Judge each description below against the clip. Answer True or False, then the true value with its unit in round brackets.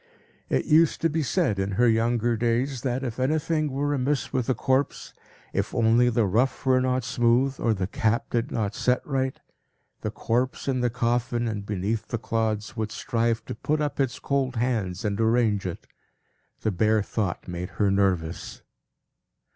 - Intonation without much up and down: False (3.2 semitones)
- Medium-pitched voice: False (120 Hz)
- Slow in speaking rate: False (175 wpm)